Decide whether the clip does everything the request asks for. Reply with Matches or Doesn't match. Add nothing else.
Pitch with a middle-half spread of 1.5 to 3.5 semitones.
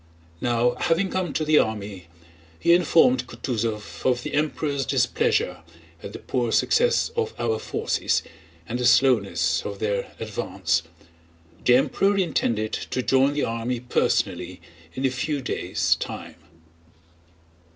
Doesn't match